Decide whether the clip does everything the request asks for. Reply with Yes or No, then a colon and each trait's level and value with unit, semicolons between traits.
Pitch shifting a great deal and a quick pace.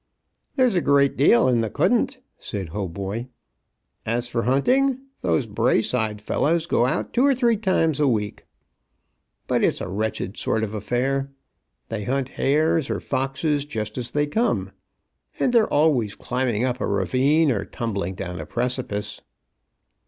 No: wide, 5.8 semitones; average, 155 wpm